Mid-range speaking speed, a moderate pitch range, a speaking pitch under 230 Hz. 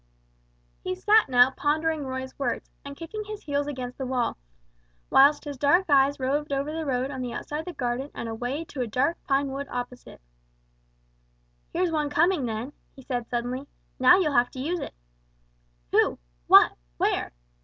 No: average, 170 wpm; average, 3.4 semitones; very high, 280 Hz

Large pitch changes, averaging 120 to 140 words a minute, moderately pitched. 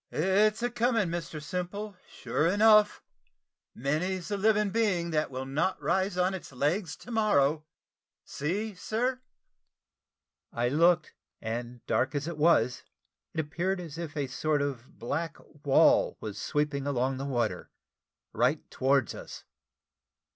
Yes: wide, 5.7 semitones; slow, 135 wpm; medium, 165 Hz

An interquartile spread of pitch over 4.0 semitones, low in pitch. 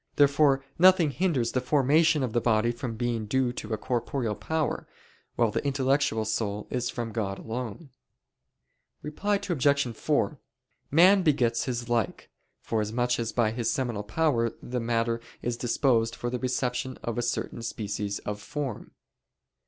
No: average, 3.5 semitones; low, 120 Hz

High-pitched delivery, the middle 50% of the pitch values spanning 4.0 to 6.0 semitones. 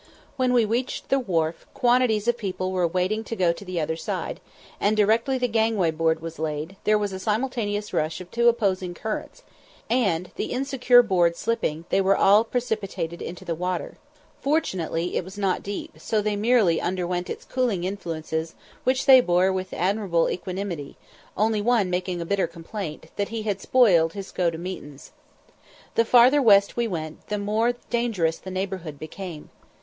Yes: high, 195 Hz; average, 4.7 semitones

